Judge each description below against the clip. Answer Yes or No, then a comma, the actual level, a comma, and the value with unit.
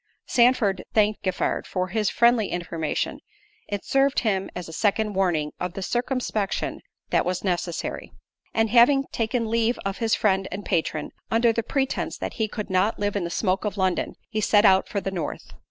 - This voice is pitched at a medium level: No, high, 205 Hz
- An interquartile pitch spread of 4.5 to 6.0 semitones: No, average, 3.5 semitones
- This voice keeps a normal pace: Yes, average, 185 wpm